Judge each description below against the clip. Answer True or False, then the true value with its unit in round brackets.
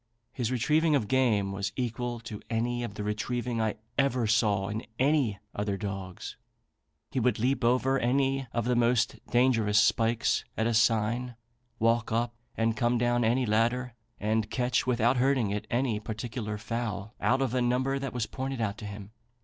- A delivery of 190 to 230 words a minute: False (175 wpm)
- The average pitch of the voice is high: False (120 Hz)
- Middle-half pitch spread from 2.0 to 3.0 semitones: True (2.7 semitones)